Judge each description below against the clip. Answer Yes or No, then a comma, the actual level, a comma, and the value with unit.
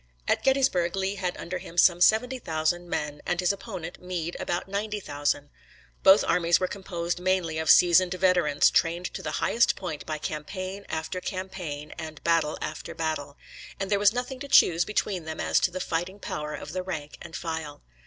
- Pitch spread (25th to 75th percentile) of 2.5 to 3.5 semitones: Yes, average, 3.1 semitones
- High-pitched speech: No, medium, 175 Hz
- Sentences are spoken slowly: No, average, 185 wpm